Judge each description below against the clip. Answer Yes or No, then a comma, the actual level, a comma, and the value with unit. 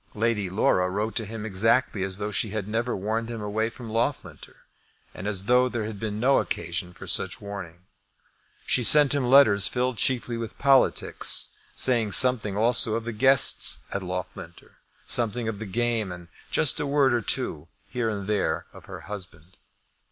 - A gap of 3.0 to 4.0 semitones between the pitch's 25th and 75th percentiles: Yes, average, 3.3 semitones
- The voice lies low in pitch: Yes, low, 110 Hz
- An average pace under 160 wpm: No, average, 175 wpm